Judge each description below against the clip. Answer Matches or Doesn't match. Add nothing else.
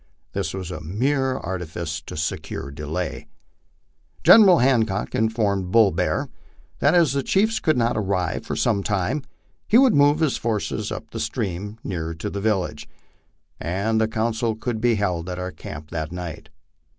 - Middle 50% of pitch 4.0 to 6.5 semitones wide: Matches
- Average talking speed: Matches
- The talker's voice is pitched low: Matches